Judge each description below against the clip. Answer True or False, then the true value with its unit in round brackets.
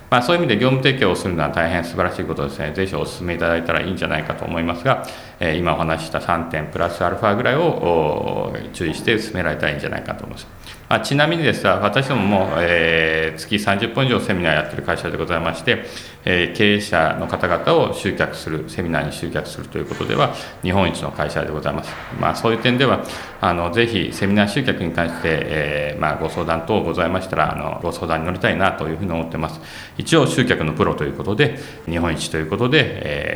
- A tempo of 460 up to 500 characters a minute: True (465 characters per minute)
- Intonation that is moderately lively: True (3.9 semitones)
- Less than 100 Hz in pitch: True (85 Hz)